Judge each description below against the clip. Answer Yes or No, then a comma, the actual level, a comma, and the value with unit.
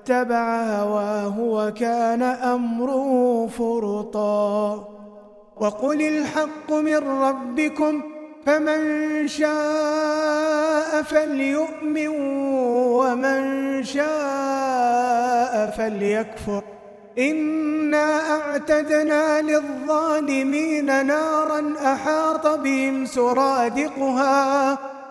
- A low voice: No, very high, 275 Hz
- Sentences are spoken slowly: Yes, slow, 55 wpm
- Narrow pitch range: No, average, 4.1 semitones